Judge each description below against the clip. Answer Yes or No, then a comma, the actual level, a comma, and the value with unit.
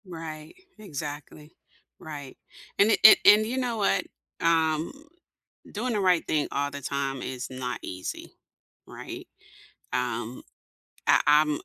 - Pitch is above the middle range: No, medium, 155 Hz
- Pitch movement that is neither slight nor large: Yes, average, 5.0 semitones